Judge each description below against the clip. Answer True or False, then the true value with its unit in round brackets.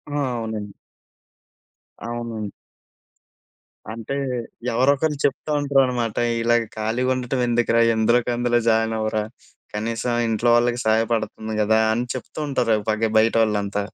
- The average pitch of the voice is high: False (115 Hz)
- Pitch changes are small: True (1.8 semitones)